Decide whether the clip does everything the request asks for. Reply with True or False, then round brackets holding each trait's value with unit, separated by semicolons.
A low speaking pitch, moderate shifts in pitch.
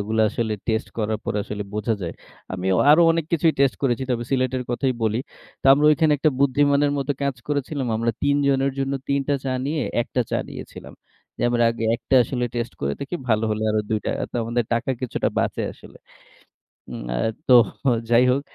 True (125 Hz; 3.8 semitones)